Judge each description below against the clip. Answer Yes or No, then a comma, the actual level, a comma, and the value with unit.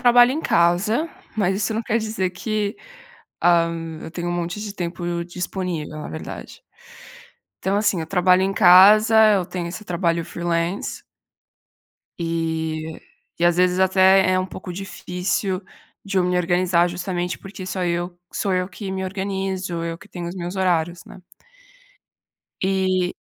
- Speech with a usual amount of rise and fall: No, narrow, 2.0 semitones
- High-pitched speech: No, medium, 180 Hz